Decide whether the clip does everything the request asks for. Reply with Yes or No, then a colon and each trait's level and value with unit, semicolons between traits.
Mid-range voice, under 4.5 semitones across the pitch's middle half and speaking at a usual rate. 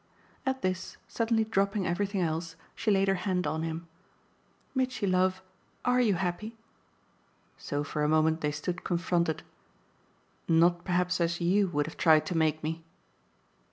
Yes: medium, 180 Hz; average, 3.3 semitones; average, 150 wpm